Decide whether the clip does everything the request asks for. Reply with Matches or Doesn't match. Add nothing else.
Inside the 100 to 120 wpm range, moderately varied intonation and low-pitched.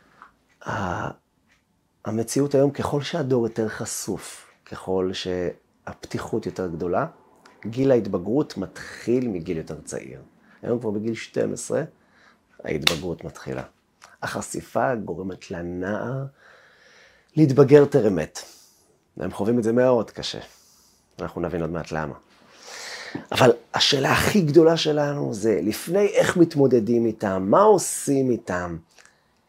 Doesn't match